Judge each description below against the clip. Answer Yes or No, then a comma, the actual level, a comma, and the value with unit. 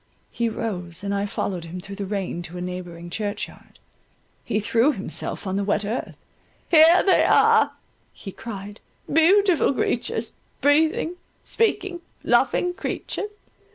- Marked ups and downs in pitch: Yes, wide, 8.6 semitones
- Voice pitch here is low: No, high, 210 Hz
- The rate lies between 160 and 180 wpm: No, slow, 135 wpm